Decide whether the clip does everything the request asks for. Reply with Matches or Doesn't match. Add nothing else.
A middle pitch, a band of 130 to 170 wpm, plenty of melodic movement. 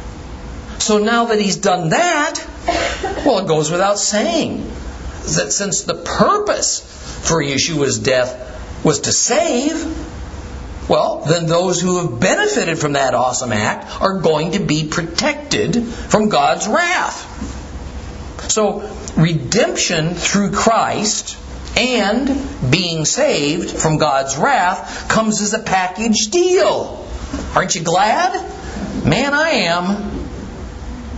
Doesn't match